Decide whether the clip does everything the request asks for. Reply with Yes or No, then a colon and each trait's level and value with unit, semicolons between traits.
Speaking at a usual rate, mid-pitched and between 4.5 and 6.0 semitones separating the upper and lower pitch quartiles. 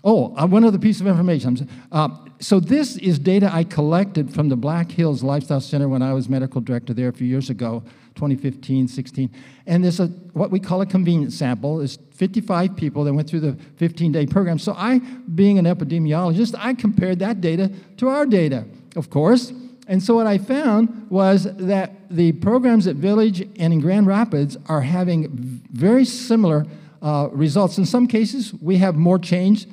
Yes: average, 185 wpm; medium, 175 Hz; wide, 5.5 semitones